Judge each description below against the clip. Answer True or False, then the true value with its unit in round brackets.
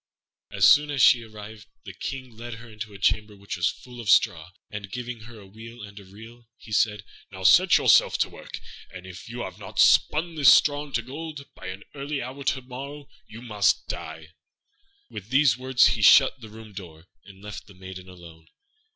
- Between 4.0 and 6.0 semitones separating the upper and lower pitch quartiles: True (4.4 semitones)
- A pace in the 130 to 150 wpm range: False (205 wpm)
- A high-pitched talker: False (110 Hz)